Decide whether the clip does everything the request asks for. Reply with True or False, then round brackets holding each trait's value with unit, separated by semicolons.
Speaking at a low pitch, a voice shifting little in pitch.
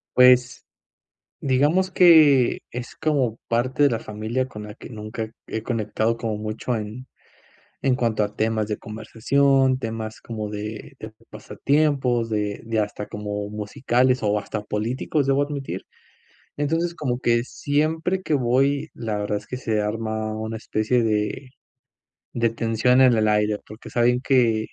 False (115 Hz; 3.5 semitones)